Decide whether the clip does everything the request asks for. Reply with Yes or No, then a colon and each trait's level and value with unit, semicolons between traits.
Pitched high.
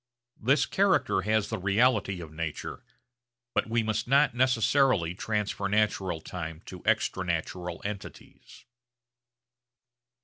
No: low, 100 Hz